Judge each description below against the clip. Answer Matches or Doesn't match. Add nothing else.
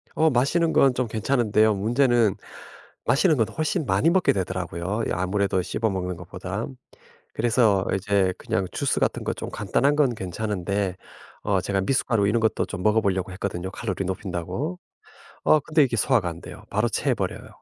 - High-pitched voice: Doesn't match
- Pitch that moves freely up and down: Doesn't match